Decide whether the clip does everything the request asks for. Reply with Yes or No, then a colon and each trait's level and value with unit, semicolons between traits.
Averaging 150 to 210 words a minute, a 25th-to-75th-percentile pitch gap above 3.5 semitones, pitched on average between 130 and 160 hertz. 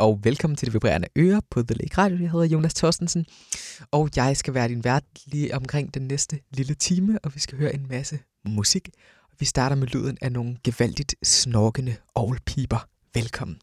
Yes: average, 190 wpm; average, 3.9 semitones; low, 135 Hz